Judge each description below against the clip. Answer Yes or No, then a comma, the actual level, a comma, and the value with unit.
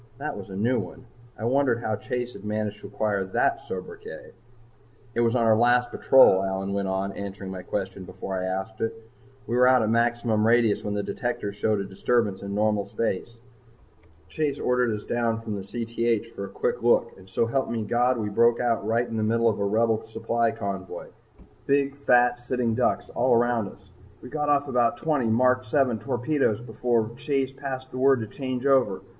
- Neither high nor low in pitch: No, low, 115 Hz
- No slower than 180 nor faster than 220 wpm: Yes, average, 195 wpm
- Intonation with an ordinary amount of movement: Yes, average, 3.2 semitones